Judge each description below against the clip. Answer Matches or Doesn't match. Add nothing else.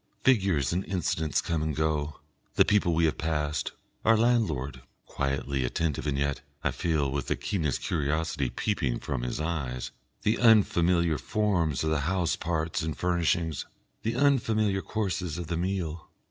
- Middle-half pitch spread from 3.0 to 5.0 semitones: Matches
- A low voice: Matches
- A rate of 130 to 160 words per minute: Matches